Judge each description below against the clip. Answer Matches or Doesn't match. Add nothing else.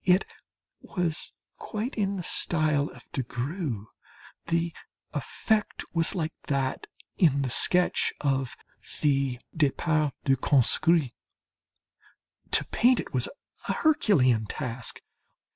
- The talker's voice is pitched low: Doesn't match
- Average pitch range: Matches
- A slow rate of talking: Matches